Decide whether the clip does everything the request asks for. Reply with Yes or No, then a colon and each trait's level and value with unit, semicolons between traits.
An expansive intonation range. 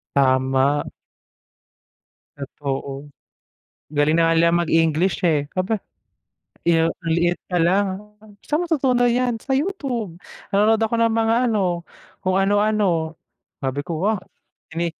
Yes: wide, 5.8 semitones